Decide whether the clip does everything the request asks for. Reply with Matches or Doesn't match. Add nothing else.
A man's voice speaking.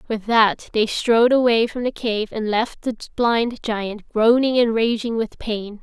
Doesn't match